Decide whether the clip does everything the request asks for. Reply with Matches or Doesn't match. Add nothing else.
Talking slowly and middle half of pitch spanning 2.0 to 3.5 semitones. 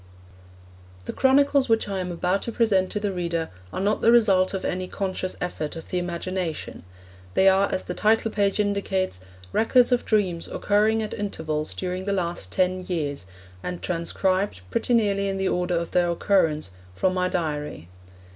Doesn't match